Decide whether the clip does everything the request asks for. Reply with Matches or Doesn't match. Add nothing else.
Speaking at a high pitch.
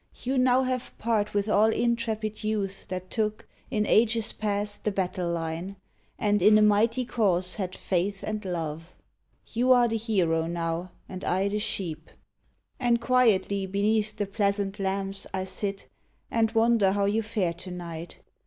Matches